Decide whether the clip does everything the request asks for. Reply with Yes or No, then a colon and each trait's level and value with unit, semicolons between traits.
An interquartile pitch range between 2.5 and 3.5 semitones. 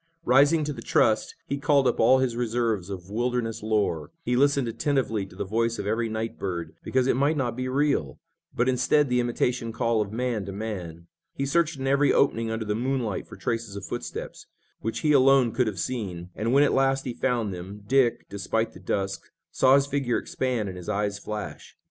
No: average, 4.1 semitones